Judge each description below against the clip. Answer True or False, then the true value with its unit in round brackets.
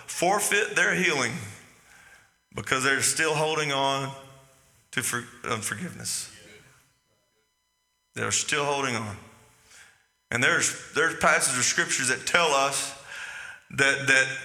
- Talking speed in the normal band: False (110 wpm)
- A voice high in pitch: False (135 Hz)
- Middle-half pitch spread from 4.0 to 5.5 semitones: False (3.6 semitones)